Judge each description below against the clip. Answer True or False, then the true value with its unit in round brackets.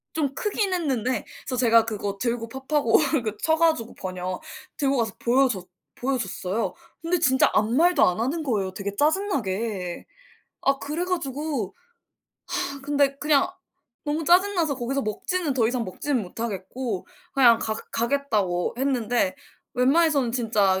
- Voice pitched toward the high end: True (255 Hz)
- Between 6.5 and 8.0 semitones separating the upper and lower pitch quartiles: False (5.3 semitones)